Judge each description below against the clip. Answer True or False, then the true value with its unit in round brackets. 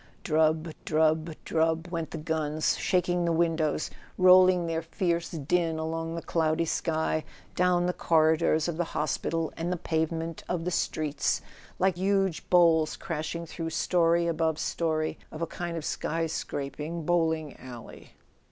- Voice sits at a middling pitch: True (165 Hz)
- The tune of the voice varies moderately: False (1.4 semitones)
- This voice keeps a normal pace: True (150 wpm)